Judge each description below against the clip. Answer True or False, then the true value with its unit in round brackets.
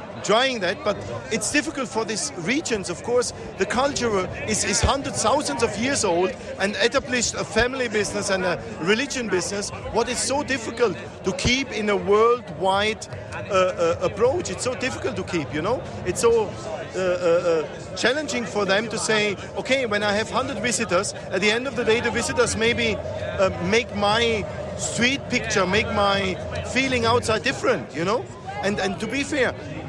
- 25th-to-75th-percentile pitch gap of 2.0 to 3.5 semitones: False (4.2 semitones)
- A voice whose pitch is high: True (220 Hz)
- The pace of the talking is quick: False (175 wpm)